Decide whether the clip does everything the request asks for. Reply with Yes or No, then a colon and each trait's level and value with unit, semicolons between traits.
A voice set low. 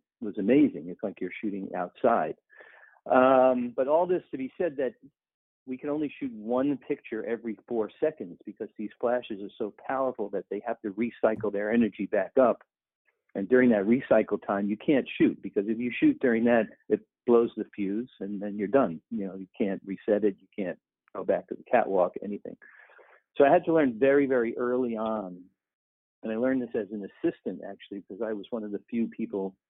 Yes: low, 115 Hz